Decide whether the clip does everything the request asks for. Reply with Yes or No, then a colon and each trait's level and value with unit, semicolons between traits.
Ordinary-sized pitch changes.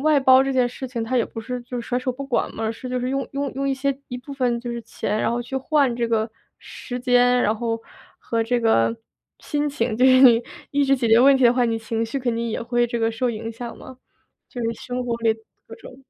No: narrow, 2.2 semitones